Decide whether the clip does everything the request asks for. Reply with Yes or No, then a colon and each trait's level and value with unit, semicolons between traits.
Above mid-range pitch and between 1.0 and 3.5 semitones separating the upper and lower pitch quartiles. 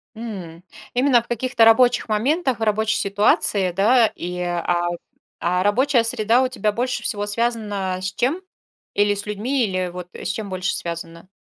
No: high, 210 Hz; average, 4.3 semitones